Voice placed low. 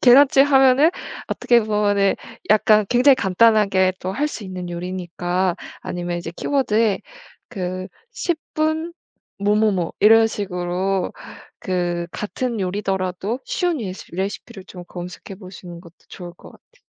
No: high, 195 Hz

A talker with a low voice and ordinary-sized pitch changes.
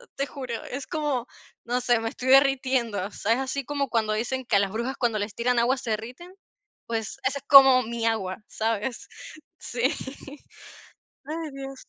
No: high, 245 Hz; average, 3.2 semitones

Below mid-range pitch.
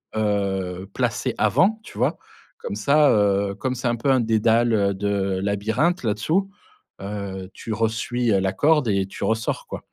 Yes: low, 105 Hz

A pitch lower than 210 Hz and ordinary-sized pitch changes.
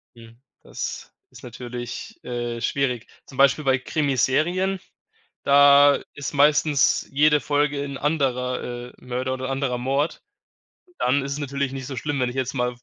No: low, 135 Hz; narrow, 2.3 semitones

